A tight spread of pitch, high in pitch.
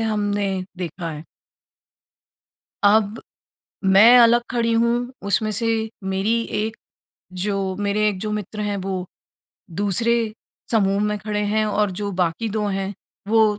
Yes: narrow, 2.2 semitones; high, 210 Hz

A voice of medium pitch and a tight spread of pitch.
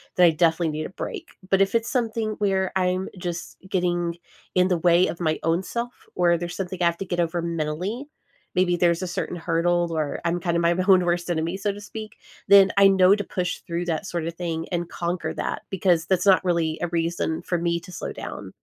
Yes: medium, 175 Hz; narrow, 2.1 semitones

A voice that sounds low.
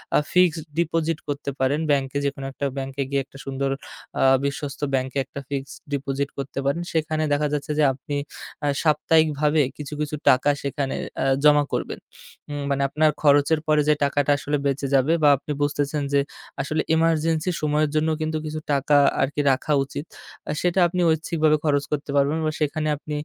No: medium, 145 Hz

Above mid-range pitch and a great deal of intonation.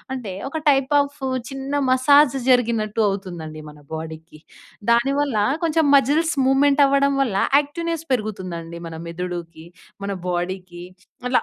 Yes: high, 235 Hz; wide, 8.1 semitones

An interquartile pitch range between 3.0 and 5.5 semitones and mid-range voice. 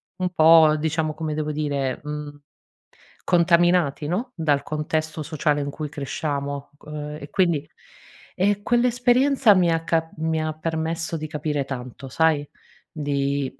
No: narrow, 2.4 semitones; medium, 155 Hz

